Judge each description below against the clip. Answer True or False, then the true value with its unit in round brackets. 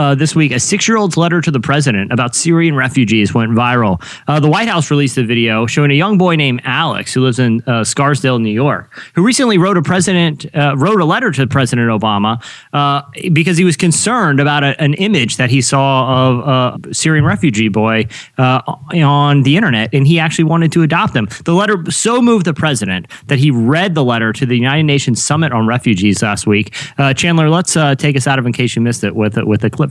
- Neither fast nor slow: False (225 wpm)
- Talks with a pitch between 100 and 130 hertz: False (140 Hz)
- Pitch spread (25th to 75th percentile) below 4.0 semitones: False (5.1 semitones)